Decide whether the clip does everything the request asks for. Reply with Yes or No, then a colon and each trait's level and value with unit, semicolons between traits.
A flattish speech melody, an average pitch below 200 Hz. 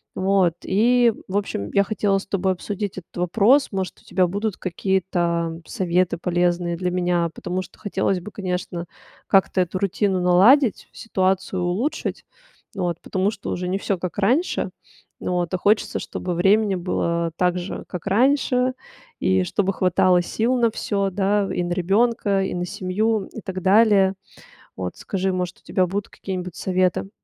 Yes: narrow, 2.3 semitones; high, 190 Hz